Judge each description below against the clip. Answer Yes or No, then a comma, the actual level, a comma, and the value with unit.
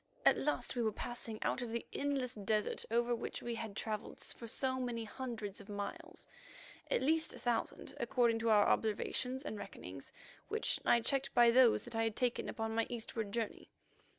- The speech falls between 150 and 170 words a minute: No, average, 185 wpm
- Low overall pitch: No, high, 235 Hz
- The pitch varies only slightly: Yes, narrow, 2.2 semitones